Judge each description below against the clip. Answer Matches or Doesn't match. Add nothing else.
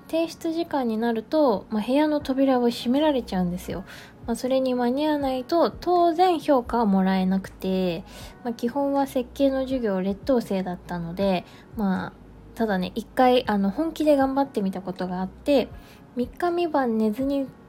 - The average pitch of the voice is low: Doesn't match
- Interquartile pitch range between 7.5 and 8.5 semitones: Doesn't match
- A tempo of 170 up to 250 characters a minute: Doesn't match